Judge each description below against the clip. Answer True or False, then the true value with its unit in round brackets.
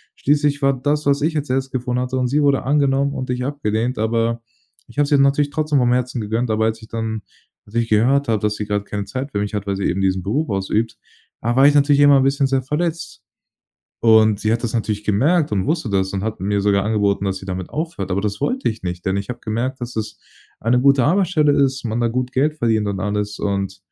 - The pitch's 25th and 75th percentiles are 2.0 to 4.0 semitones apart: False (5.1 semitones)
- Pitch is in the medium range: False (120 Hz)